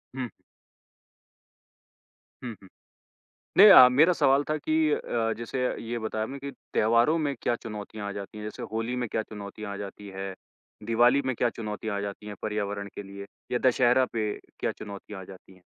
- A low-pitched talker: Yes, low, 110 Hz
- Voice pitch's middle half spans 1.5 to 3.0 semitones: No, average, 3.7 semitones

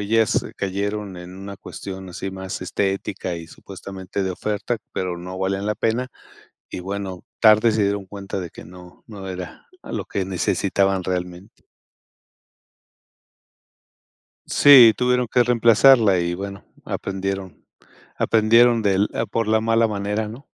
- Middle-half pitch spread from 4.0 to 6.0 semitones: No, average, 2.7 semitones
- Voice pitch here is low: Yes, low, 100 Hz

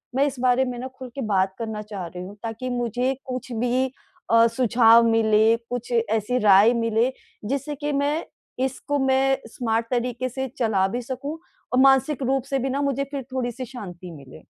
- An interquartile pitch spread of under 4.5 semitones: Yes, average, 2.9 semitones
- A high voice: Yes, high, 245 Hz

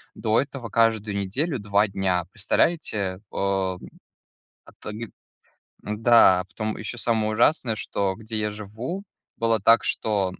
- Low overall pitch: Yes, low, 110 Hz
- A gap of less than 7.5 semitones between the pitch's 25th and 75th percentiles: Yes, narrow, 2.4 semitones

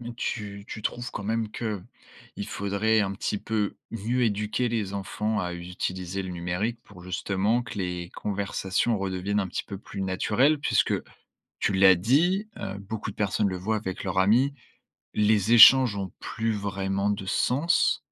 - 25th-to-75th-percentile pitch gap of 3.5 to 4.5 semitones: No, average, 2.7 semitones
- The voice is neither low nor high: No, low, 100 Hz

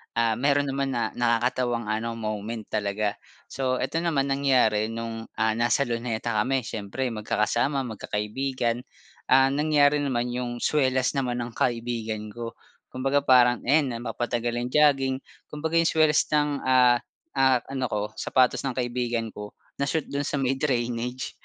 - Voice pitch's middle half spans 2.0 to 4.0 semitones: Yes, average, 2.9 semitones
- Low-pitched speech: Yes, low, 125 Hz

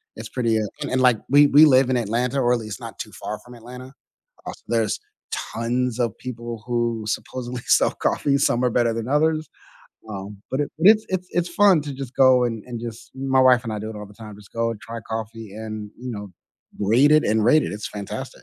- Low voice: Yes, low, 120 Hz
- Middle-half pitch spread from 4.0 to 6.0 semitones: No, average, 2.9 semitones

